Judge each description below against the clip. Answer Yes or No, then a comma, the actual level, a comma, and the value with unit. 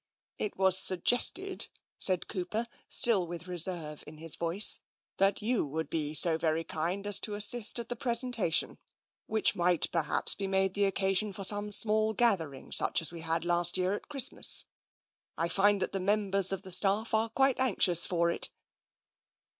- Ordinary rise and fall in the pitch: Yes, average, 3.8 semitones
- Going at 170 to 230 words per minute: Yes, average, 180 wpm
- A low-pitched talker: No, high, 190 Hz